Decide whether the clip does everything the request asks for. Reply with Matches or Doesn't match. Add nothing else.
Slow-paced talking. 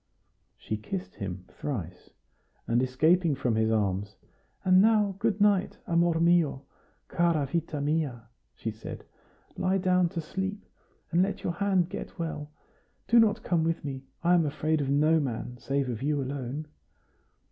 Doesn't match